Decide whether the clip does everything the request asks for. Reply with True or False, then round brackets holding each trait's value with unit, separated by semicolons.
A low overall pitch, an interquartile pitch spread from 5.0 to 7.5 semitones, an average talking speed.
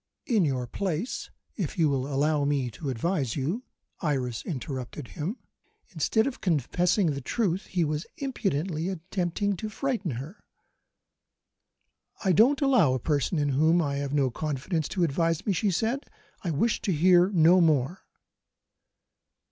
False (165 Hz; 5.3 semitones; 150 wpm)